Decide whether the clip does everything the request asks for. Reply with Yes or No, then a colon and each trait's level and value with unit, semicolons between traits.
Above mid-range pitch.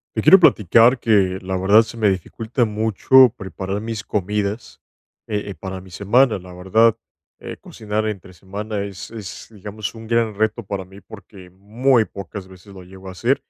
No: low, 105 Hz